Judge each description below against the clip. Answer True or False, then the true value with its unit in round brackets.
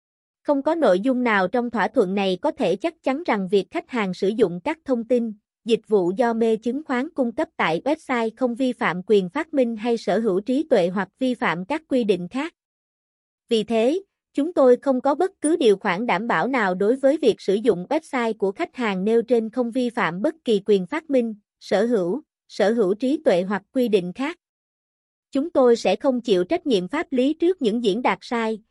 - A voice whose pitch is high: True (240 Hz)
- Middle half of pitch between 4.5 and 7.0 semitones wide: True (4.9 semitones)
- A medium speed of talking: True (220 wpm)